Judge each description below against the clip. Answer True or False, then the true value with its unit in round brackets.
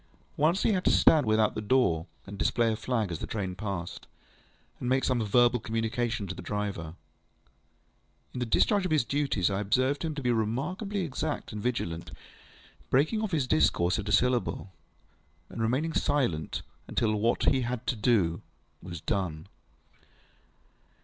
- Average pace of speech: True (165 wpm)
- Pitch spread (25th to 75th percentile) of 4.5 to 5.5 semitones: True (5.0 semitones)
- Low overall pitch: True (115 Hz)